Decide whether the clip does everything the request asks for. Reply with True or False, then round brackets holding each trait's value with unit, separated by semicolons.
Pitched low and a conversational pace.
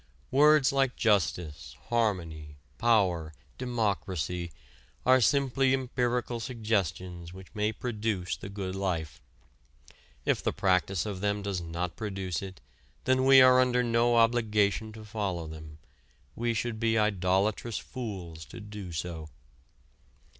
False (105 Hz; 125 wpm)